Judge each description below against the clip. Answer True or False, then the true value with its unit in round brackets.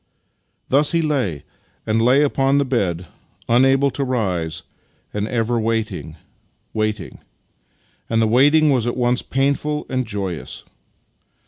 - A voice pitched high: False (120 Hz)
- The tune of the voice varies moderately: True (4.1 semitones)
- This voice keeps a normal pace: False (130 wpm)